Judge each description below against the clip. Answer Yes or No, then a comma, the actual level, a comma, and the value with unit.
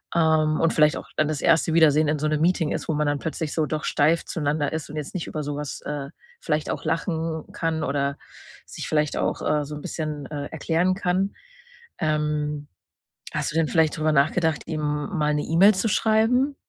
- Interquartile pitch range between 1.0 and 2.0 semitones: Yes, narrow, 1.7 semitones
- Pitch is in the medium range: Yes, medium, 155 Hz